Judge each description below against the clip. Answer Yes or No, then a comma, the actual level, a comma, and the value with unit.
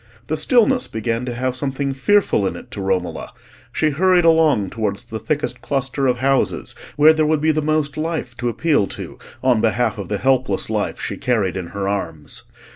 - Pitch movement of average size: No, wide, 5.9 semitones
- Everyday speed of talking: Yes, average, 195 wpm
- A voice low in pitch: Yes, low, 130 Hz